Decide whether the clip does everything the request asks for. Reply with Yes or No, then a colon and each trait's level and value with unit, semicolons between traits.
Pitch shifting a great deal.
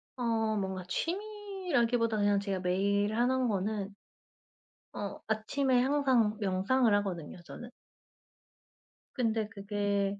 No: average, 3.8 semitones